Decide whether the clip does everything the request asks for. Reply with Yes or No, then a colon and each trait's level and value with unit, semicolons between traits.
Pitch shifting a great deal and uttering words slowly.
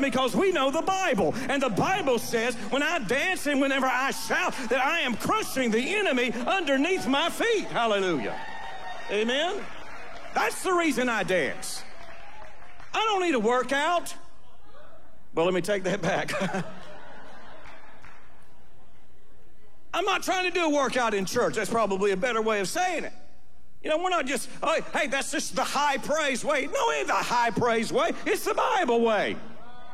No: wide, 6.7 semitones; average, 170 wpm